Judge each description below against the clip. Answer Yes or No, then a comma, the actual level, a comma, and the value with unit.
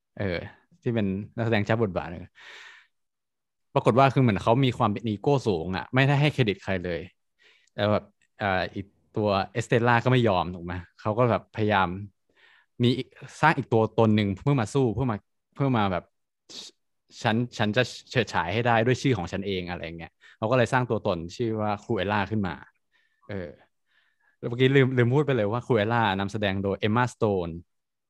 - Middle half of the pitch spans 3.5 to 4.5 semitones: Yes, average, 4.0 semitones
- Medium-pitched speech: No, low, 110 Hz